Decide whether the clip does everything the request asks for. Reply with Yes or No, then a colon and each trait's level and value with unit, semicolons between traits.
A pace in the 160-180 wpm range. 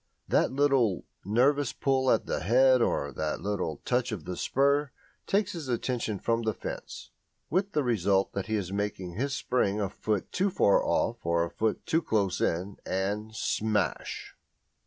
Yes: average, 165 wpm